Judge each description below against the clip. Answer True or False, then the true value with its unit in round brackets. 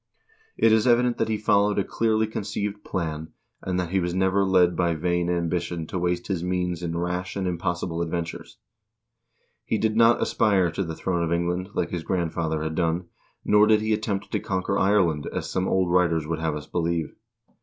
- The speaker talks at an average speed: True (195 wpm)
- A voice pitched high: False (90 Hz)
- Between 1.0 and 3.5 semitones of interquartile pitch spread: True (2.8 semitones)